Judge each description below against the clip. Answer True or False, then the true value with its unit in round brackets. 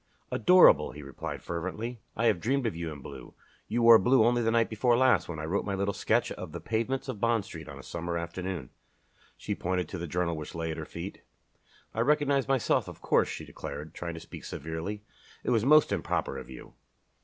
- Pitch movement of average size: False (6.1 semitones)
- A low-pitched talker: True (100 Hz)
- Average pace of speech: False (215 wpm)